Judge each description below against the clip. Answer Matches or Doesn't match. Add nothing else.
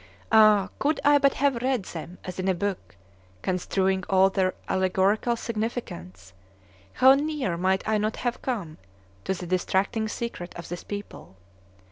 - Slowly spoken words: Doesn't match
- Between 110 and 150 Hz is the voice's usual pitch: Doesn't match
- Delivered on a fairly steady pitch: Doesn't match